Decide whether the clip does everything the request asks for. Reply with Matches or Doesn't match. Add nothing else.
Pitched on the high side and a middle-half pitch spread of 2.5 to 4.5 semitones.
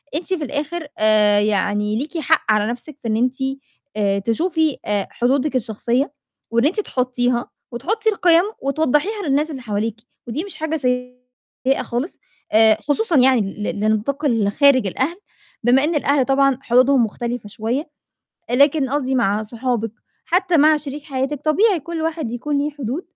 Doesn't match